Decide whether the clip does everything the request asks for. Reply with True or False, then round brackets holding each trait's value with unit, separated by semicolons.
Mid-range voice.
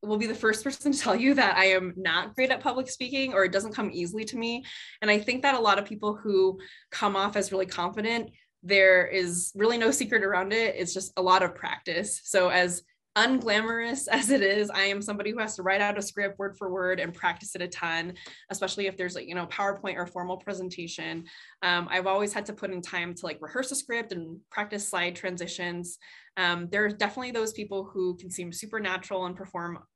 False (195 Hz)